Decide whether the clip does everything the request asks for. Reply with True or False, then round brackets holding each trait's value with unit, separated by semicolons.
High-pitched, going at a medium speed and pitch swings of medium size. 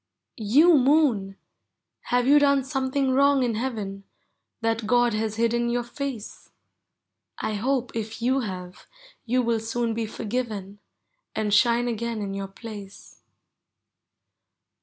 False (235 Hz; 125 wpm; 3.4 semitones)